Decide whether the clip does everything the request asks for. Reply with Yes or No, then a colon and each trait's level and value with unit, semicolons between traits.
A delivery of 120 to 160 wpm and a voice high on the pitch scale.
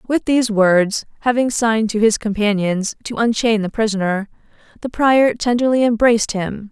Yes: average, 150 wpm; high, 220 Hz